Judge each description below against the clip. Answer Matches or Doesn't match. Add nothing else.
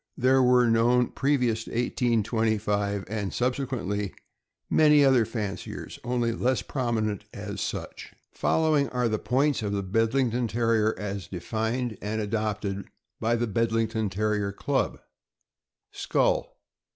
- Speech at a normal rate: Doesn't match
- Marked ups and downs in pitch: Doesn't match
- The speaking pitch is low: Matches